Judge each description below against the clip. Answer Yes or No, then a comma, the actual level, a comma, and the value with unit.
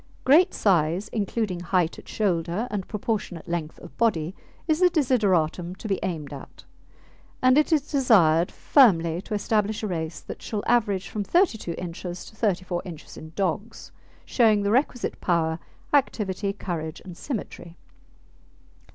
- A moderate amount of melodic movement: Yes, average, 4.7 semitones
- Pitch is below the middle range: No, high, 195 Hz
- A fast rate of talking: No, average, 145 wpm